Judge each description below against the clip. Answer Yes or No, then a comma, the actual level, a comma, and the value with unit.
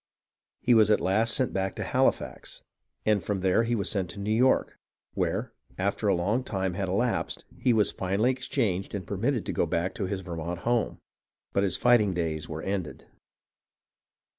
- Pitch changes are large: No, average, 3.3 semitones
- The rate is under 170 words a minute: No, average, 175 wpm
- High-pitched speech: No, low, 100 Hz